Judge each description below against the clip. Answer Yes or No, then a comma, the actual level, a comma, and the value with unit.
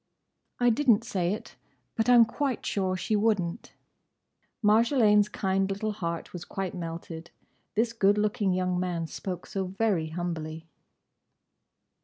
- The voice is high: Yes, high, 195 Hz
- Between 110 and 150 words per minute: Yes, slow, 135 wpm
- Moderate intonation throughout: Yes, average, 3.7 semitones